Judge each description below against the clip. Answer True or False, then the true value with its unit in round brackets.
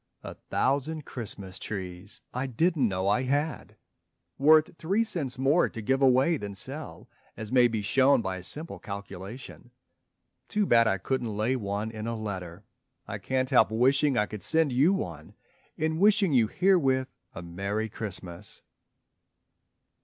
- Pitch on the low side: True (125 Hz)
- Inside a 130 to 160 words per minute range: True (155 wpm)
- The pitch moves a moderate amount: False (5.9 semitones)